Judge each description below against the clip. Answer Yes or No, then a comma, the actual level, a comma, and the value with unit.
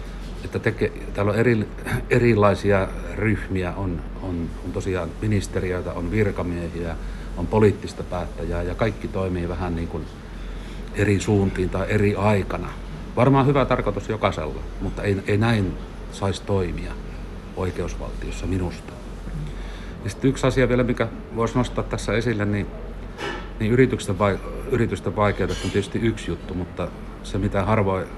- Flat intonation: No, average, 3.4 semitones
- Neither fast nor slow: Yes, average, 135 wpm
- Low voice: Yes, very low, 95 Hz